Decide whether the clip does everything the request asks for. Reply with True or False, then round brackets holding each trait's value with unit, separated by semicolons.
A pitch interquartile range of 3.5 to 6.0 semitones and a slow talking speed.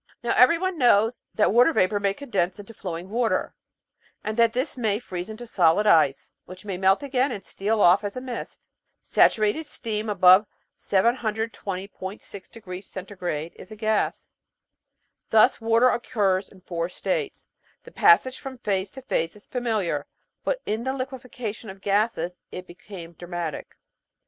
False (4.3 semitones; 145 wpm)